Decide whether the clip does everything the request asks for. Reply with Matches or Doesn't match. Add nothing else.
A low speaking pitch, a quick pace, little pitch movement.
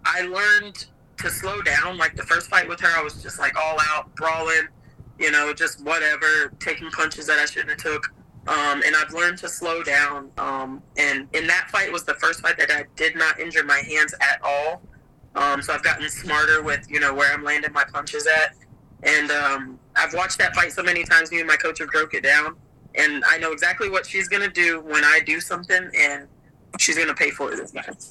Doesn't match